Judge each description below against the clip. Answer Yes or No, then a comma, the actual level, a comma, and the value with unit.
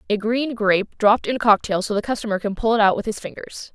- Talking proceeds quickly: Yes, fast, 275 wpm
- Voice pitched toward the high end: Yes, high, 220 Hz